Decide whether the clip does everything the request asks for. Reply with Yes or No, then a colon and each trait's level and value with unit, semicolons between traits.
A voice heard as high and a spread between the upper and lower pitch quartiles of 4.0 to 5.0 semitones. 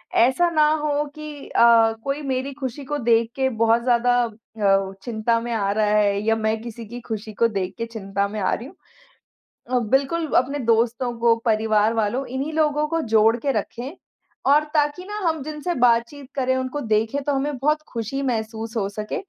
Yes: high, 240 Hz; average, 4.3 semitones